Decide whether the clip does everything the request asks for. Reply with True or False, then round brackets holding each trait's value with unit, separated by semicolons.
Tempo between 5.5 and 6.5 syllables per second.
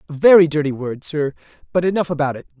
False (6.8 syllables/s)